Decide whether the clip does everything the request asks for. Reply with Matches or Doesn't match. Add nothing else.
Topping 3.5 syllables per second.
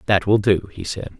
Matches